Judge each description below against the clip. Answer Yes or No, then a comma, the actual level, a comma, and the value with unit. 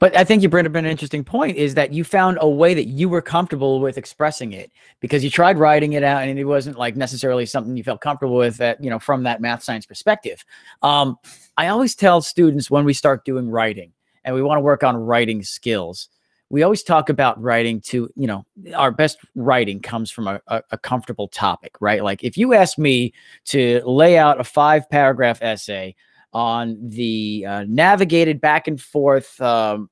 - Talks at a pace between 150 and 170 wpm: No, fast, 205 wpm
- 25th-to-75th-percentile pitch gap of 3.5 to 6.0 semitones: Yes, average, 4.5 semitones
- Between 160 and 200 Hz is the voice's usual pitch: No, low, 135 Hz